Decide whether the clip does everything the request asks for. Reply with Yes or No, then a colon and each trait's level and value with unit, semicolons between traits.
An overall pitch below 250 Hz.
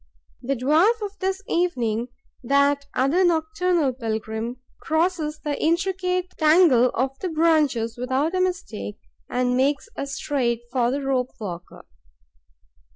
No: very high, 280 Hz